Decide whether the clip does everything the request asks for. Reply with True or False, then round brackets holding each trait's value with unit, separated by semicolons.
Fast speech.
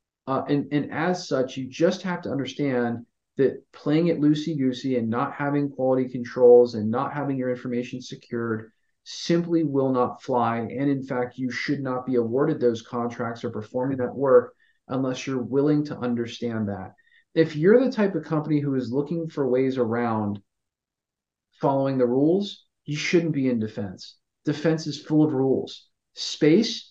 False (170 wpm)